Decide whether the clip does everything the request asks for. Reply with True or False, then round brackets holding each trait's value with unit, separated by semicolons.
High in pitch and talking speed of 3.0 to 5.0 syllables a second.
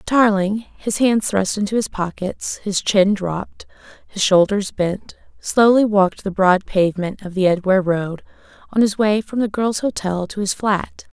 True (200 Hz; 4.5 syllables/s)